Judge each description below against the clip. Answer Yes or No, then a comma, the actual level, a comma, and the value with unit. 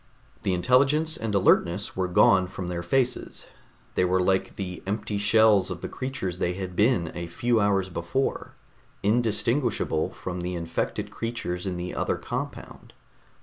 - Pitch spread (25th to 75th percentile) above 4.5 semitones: No, average, 4.2 semitones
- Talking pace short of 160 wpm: Yes, average, 150 wpm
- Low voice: Yes, very low, 95 Hz